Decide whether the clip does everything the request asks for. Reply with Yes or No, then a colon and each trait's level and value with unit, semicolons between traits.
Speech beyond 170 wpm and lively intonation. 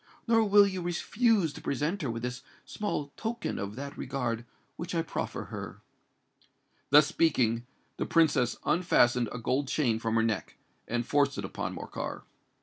No: average, 160 wpm; wide, 6.4 semitones